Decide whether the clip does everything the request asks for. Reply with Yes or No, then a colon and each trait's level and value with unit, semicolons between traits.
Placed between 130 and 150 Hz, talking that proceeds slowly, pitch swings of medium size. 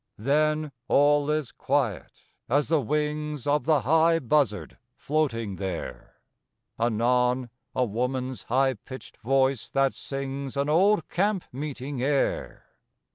Yes: low, 135 Hz; slow, 120 wpm; average, 3.2 semitones